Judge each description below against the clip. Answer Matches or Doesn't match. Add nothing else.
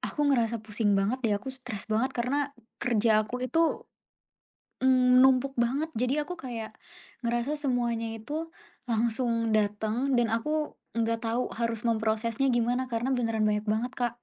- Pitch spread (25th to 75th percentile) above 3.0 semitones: Doesn't match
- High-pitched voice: Matches